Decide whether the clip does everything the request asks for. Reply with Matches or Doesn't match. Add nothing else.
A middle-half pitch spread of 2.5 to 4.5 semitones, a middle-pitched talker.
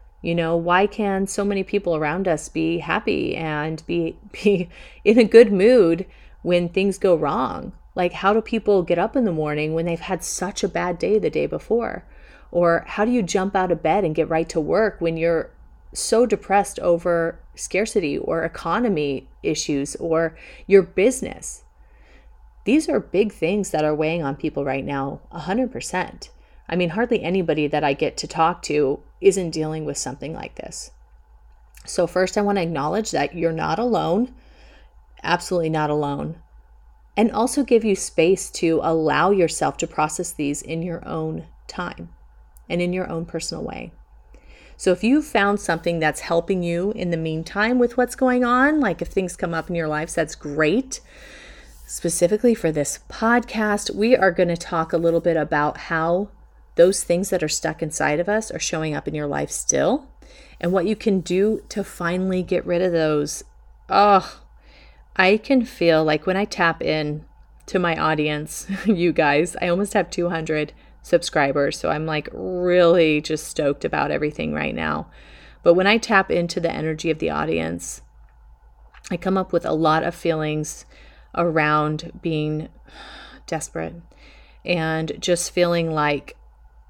Matches